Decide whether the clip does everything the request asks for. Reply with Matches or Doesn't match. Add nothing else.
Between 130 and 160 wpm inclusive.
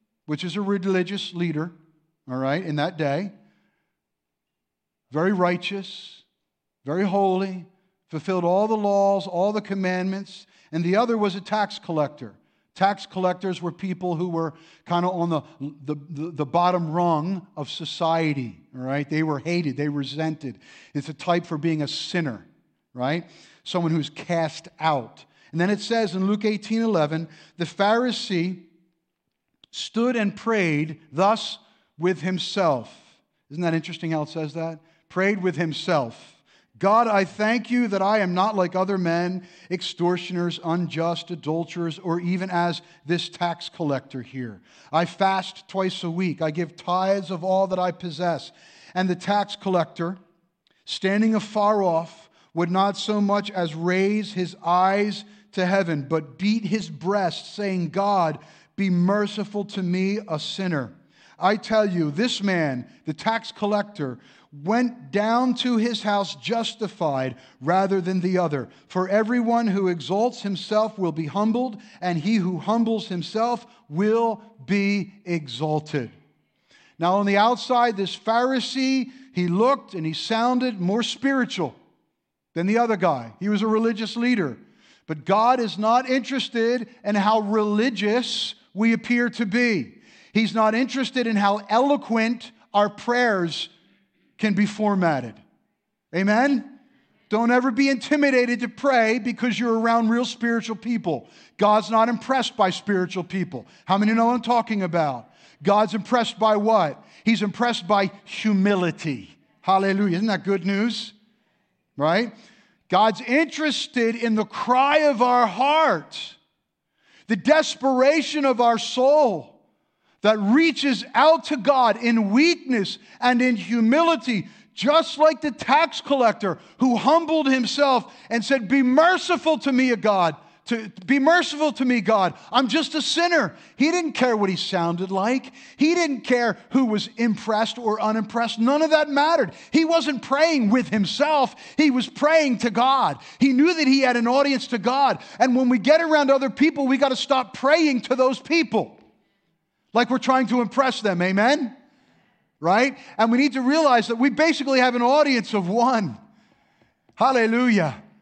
Matches